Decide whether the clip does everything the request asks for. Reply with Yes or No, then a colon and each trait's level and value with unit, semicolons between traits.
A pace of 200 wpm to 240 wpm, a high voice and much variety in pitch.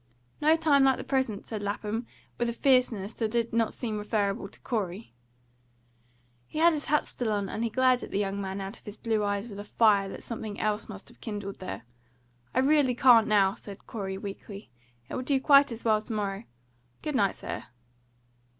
No: fast, 205 wpm; high, 220 Hz; average, 3.8 semitones